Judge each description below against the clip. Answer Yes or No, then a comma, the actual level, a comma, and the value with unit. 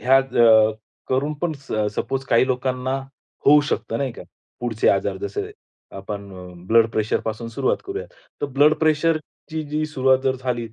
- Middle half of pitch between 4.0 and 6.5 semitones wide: Yes, average, 4.3 semitones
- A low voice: Yes, low, 130 Hz